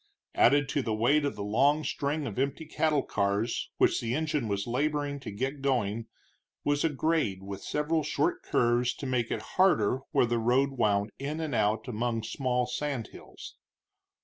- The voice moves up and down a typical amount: Yes, average, 4.5 semitones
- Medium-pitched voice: No, low, 130 Hz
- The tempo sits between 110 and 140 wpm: No, average, 175 wpm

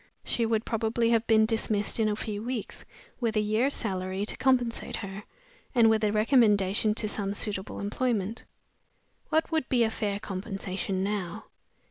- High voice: Yes, high, 215 Hz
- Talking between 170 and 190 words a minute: No, average, 160 wpm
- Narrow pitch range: Yes, narrow, 2.3 semitones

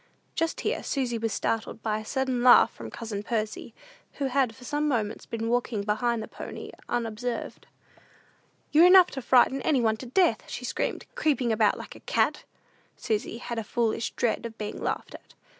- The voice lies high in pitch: Yes, high, 235 Hz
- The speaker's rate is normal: Yes, average, 180 wpm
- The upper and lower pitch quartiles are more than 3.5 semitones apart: No, average, 3.1 semitones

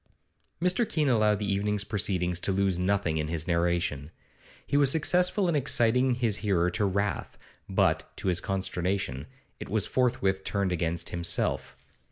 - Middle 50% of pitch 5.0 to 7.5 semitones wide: Yes, wide, 5.4 semitones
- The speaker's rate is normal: Yes, average, 155 wpm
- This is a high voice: No, low, 100 Hz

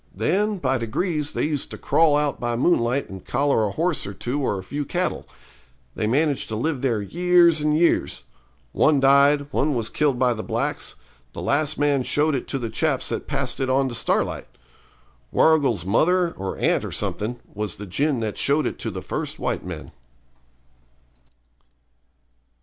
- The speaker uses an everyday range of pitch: Yes, average, 4.5 semitones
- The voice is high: No, medium, 140 Hz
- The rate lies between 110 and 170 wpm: No, average, 180 wpm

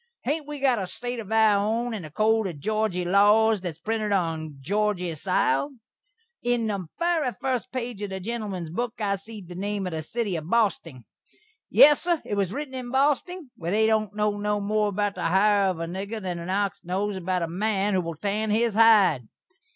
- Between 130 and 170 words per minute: No, fast, 205 wpm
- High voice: Yes, high, 205 Hz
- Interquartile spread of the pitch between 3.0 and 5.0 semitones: Yes, average, 3.5 semitones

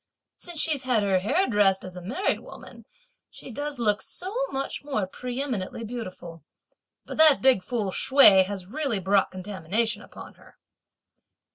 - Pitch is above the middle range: Yes, high, 220 Hz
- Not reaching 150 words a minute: No, average, 155 wpm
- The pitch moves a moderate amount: No, wide, 5.9 semitones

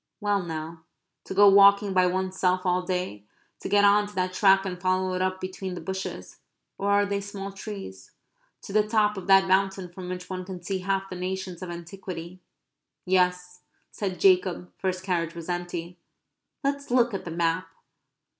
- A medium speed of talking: Yes, average, 185 wpm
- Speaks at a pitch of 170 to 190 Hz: Yes, medium, 185 Hz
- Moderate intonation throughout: No, narrow, 1.5 semitones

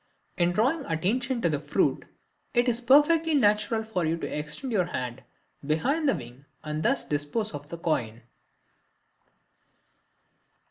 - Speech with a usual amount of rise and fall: No, wide, 8.3 semitones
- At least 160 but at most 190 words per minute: No, average, 140 wpm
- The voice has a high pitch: No, medium, 180 Hz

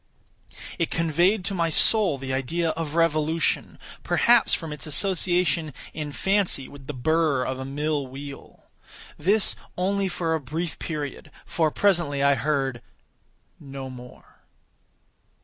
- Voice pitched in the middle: Yes, medium, 155 Hz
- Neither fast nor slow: No, slow, 130 wpm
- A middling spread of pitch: Yes, average, 3.7 semitones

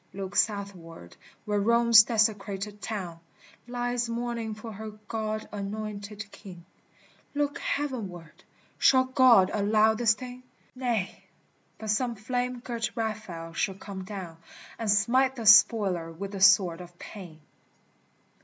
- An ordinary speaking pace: No, slow, 125 wpm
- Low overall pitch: No, high, 215 Hz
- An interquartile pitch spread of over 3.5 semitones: No, average, 3.2 semitones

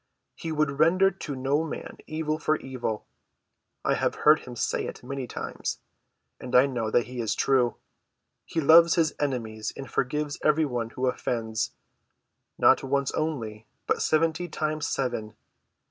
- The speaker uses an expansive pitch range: No, average, 4.2 semitones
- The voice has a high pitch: No, low, 135 Hz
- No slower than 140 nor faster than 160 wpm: Yes, average, 150 wpm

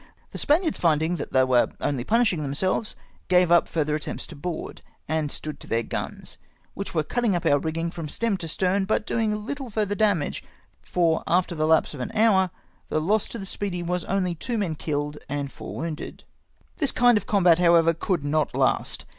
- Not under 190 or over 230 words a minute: Yes, average, 195 wpm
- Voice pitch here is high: No, medium, 175 Hz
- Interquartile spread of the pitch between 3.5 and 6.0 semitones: Yes, average, 4.9 semitones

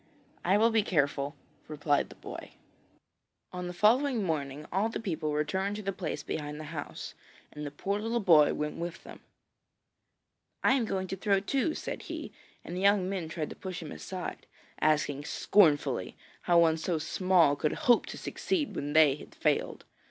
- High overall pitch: No, medium, 175 Hz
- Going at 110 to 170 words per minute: No, average, 180 wpm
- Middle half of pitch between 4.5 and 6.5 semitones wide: Yes, average, 4.9 semitones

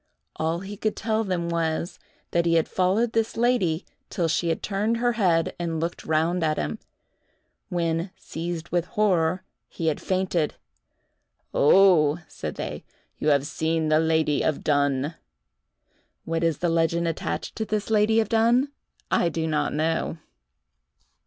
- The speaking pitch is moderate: Yes, medium, 170 Hz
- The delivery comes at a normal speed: Yes, average, 150 wpm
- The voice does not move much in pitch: No, average, 3.6 semitones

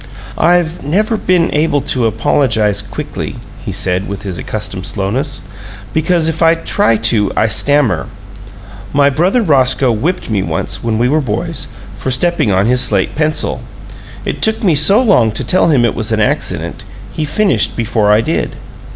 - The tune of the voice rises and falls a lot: Yes, wide, 7.0 semitones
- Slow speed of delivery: No, average, 170 wpm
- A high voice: No, low, 130 Hz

